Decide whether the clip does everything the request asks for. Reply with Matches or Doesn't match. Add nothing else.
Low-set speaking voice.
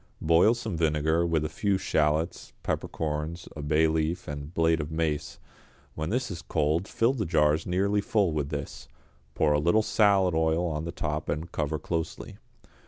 Matches